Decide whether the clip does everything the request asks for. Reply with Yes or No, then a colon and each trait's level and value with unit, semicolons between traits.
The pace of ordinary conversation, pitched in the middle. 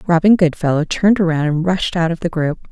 No: fast, 220 wpm; medium, 170 Hz